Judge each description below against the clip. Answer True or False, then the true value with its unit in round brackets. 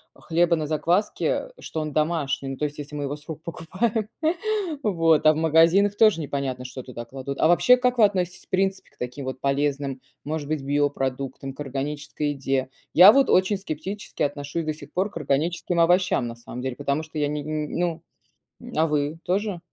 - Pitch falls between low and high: True (155 Hz)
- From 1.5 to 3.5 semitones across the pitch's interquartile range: False (3.9 semitones)